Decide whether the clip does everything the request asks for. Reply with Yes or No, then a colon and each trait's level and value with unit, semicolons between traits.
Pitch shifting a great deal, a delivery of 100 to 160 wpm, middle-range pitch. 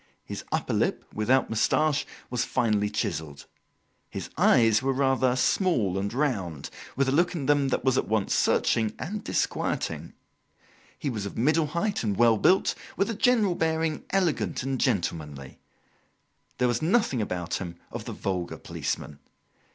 No: wide, 7.3 semitones; average, 155 wpm; low, 125 Hz